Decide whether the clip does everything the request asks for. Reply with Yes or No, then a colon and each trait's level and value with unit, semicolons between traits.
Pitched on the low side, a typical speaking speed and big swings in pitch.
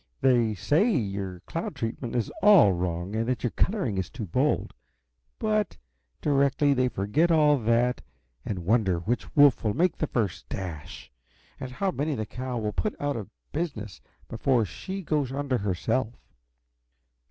Yes: low, 125 Hz; average, 155 wpm; wide, 5.9 semitones